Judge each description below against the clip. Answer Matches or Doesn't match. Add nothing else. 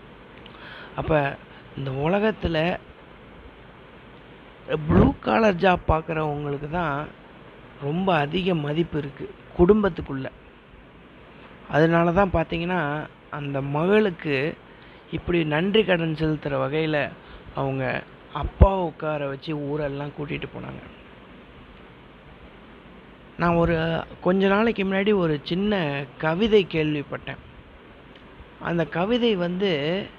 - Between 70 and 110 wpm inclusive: Matches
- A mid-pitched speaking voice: Matches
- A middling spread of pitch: Matches